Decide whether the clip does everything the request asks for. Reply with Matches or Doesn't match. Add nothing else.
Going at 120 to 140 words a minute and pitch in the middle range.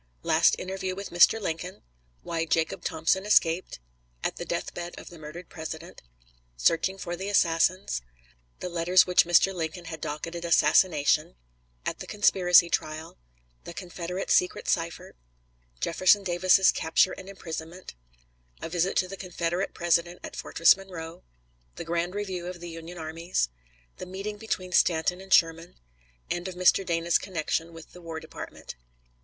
Doesn't match